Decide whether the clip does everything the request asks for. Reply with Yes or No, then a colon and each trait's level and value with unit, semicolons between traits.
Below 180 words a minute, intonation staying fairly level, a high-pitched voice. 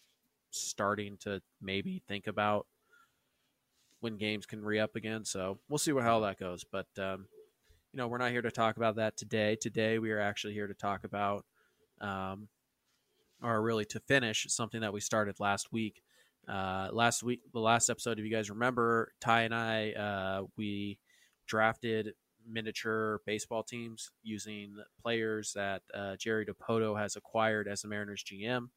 No: average, 165 wpm; narrow, 2.1 semitones; low, 110 Hz